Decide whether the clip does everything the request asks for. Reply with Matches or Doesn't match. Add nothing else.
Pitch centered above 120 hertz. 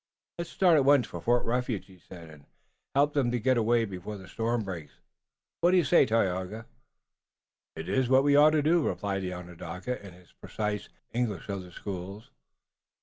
Doesn't match